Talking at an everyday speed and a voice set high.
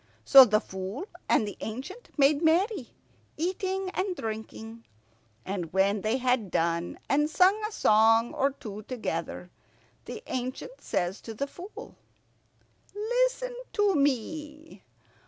No: slow, 125 wpm; very high, 265 Hz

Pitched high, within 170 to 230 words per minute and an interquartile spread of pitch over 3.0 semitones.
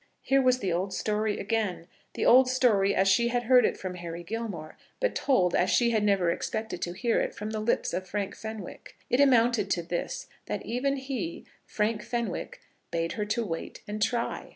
Yes: high, 215 Hz; average, 195 wpm; average, 4.3 semitones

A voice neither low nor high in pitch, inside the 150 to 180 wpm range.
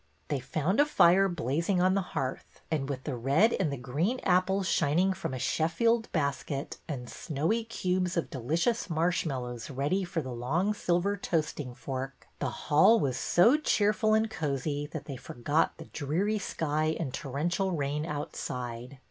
Yes: medium, 160 Hz; average, 160 wpm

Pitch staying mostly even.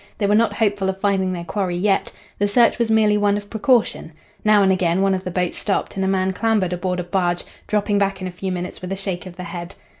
Yes: narrow, 2.2 semitones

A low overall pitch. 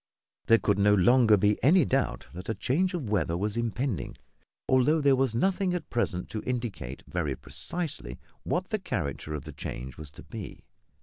Yes: low, 115 Hz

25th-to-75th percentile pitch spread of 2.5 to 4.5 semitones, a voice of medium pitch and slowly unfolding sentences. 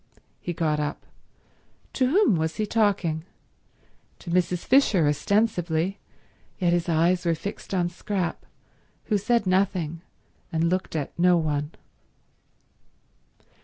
Yes: average, 3.6 semitones; medium, 175 Hz; slow, 120 wpm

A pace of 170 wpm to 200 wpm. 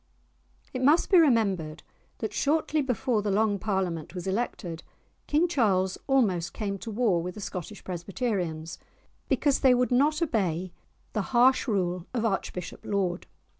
No: average, 145 wpm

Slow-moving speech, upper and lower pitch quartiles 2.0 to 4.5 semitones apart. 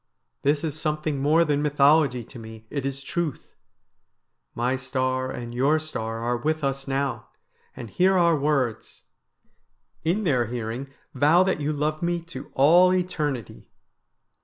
No: average, 145 wpm; average, 3.4 semitones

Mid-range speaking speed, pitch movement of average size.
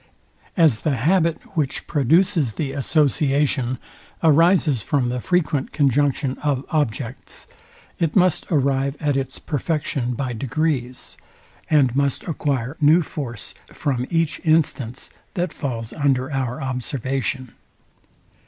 No: slow, 115 wpm; average, 3.3 semitones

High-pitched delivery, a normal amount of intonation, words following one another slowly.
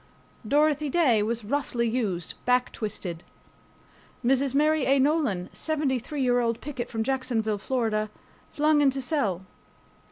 Yes: very high, 255 Hz; average, 4.6 semitones; slow, 125 wpm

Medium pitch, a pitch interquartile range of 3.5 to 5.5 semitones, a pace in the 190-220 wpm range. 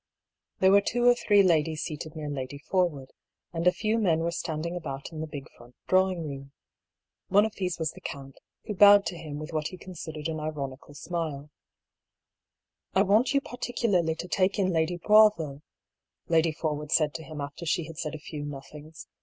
Yes: medium, 160 Hz; average, 3.8 semitones; average, 195 wpm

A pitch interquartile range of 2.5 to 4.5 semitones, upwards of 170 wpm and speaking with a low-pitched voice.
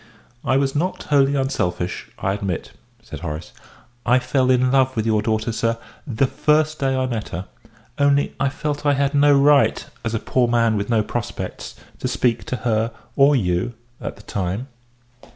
Yes: average, 4.2 semitones; average, 180 wpm; low, 125 Hz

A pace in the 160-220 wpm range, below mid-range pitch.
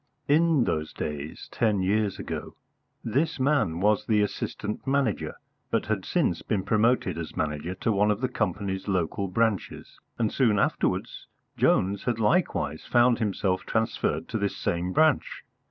No: average, 150 wpm; low, 105 Hz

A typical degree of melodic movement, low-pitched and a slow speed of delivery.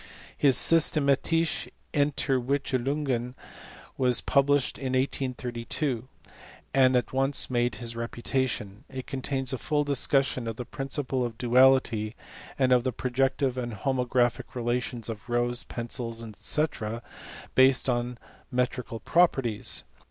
No: narrow, 2.1 semitones; low, 125 Hz; slow, 115 wpm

